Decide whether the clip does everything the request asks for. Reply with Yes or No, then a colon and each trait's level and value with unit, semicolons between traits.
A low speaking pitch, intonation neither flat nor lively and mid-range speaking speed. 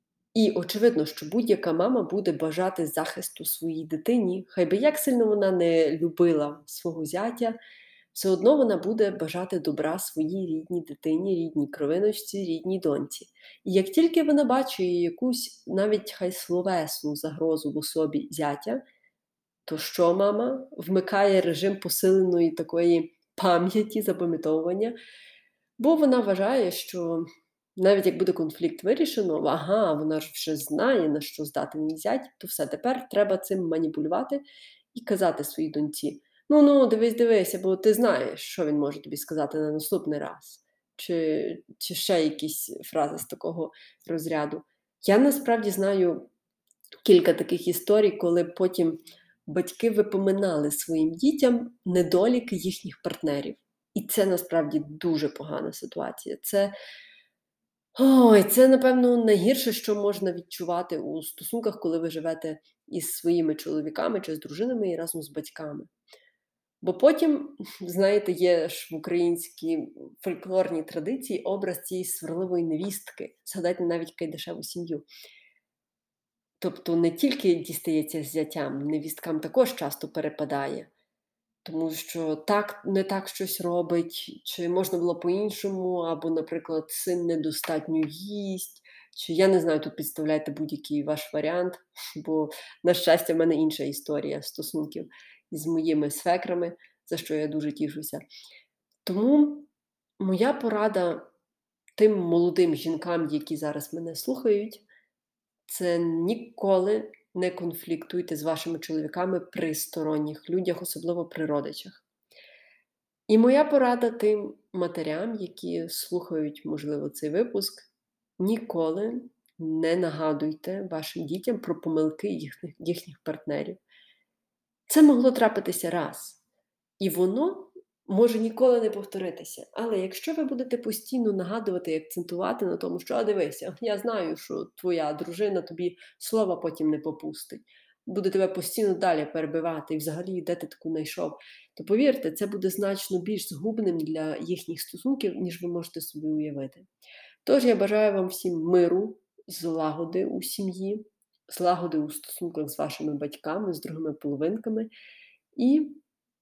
No: medium, 180 Hz; average, 4.7 semitones; average, 130 wpm